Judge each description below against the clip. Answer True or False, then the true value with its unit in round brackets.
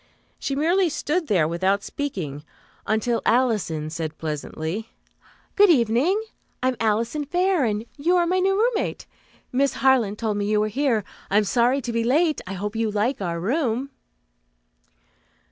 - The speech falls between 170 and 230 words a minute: False (155 wpm)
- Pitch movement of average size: False (6.1 semitones)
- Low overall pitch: False (230 Hz)